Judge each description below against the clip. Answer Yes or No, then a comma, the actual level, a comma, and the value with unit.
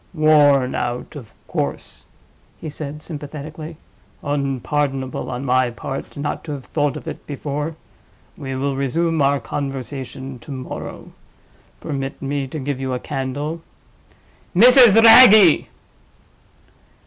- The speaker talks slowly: Yes, slow, 120 wpm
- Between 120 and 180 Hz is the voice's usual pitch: Yes, medium, 140 Hz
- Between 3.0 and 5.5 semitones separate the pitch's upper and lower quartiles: No, narrow, 2.5 semitones